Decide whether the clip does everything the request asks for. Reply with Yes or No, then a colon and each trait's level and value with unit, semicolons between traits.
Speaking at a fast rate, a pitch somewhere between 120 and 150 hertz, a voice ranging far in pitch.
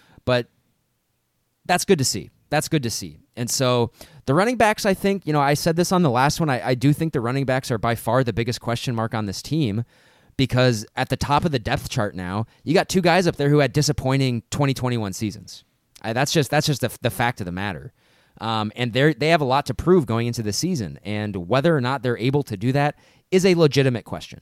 No: fast, 240 wpm; low, 130 Hz; average, 4.5 semitones